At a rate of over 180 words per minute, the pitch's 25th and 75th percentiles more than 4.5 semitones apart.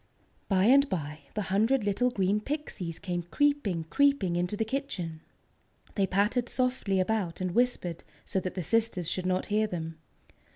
No: average, 160 wpm; average, 5.3 semitones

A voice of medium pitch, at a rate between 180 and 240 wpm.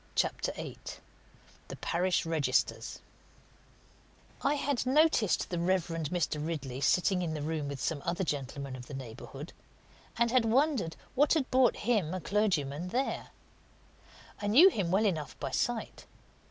No: medium, 175 Hz; average, 145 wpm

